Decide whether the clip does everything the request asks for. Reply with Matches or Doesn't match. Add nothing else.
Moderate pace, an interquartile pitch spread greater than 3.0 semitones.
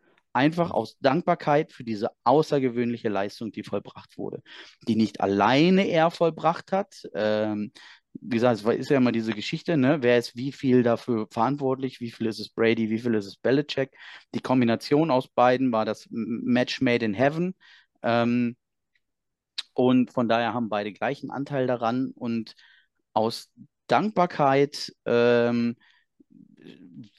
Matches